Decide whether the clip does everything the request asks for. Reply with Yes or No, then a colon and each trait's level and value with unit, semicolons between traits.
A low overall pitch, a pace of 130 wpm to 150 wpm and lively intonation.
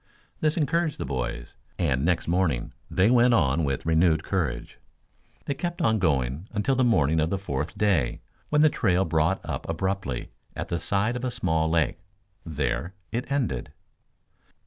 No: very low, 85 Hz; average, 165 wpm; wide, 7.0 semitones